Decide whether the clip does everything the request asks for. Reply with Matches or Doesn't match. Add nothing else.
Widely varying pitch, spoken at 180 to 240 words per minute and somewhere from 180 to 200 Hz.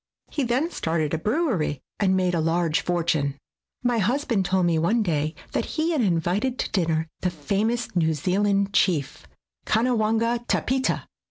Doesn't match